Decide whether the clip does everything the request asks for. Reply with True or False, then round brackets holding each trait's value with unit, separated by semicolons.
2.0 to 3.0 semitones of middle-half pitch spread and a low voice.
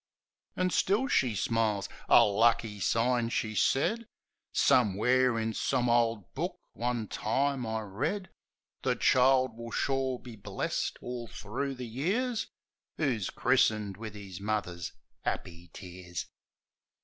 False (3.7 semitones; 115 Hz)